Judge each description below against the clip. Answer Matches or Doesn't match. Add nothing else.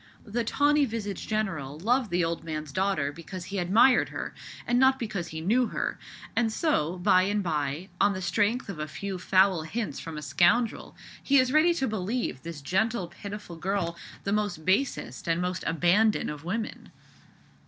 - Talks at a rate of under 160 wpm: Doesn't match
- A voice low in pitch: Doesn't match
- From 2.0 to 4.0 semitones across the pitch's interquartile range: Doesn't match